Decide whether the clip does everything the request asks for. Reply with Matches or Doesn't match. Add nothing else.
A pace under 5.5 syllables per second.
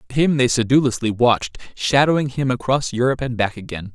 Doesn't match